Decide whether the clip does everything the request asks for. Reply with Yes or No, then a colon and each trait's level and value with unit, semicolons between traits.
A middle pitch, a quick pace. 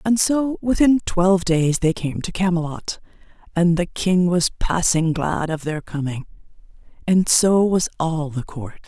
No: medium, 175 Hz; average, 160 wpm